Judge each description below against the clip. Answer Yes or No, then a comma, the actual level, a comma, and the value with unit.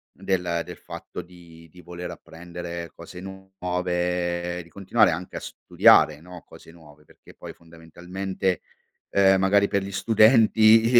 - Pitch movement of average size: No, narrow, 2.0 semitones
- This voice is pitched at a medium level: No, very low, 90 Hz